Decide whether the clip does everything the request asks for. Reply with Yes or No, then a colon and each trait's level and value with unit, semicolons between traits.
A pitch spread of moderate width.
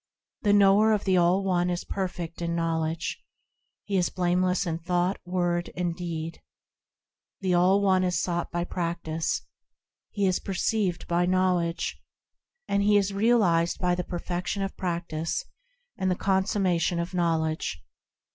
No: narrow, 2.0 semitones